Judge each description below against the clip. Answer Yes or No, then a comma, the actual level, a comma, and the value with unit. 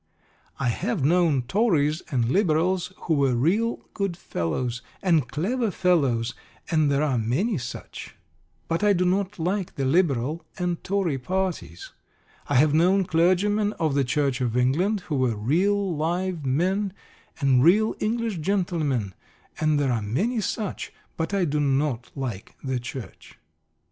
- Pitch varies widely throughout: Yes, wide, 6.2 semitones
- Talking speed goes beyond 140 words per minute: Yes, average, 150 wpm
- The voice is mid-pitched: Yes, medium, 160 Hz